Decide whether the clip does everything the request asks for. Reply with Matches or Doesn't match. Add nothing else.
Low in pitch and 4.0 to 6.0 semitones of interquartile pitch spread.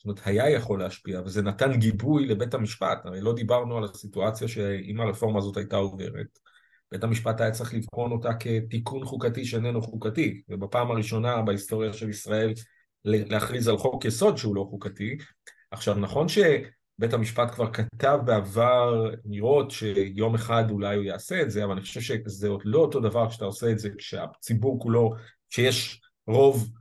Doesn't match